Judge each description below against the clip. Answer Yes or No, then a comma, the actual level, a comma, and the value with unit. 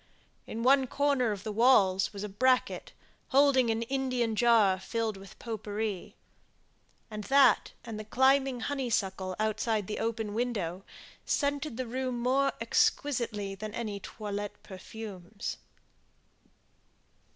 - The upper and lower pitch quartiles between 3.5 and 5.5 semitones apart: Yes, average, 3.8 semitones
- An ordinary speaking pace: No, slow, 125 wpm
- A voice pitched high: Yes, high, 225 Hz